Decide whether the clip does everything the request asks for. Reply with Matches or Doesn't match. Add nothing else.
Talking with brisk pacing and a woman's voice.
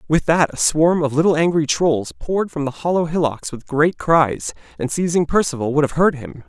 Doesn't match